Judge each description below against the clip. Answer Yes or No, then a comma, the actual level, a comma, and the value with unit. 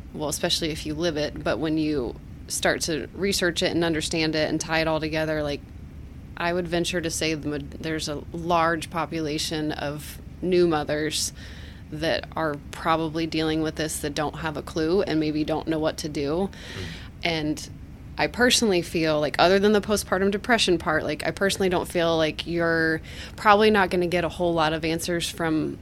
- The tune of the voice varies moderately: No, narrow, 2.2 semitones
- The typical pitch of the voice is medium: Yes, medium, 160 Hz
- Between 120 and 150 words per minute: No, average, 190 wpm